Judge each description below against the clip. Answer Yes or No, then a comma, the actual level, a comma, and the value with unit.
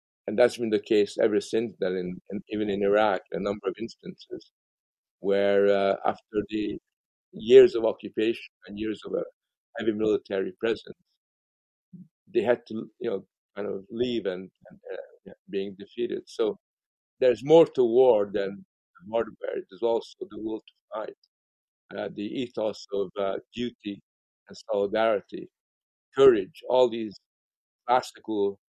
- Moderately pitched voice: No, low, 115 Hz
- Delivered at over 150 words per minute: No, average, 145 wpm